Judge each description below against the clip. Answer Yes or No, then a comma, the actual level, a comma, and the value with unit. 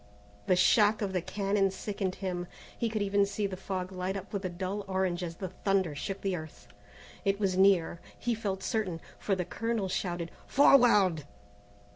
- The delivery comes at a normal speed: Yes, average, 180 wpm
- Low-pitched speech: No, high, 190 Hz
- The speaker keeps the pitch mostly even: Yes, narrow, 1.9 semitones